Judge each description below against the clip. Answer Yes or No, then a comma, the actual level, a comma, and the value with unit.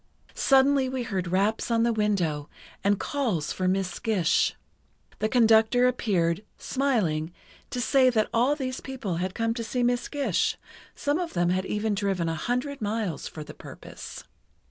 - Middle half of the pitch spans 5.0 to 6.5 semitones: Yes, average, 5.3 semitones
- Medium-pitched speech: No, high, 220 Hz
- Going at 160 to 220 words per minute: Yes, average, 165 wpm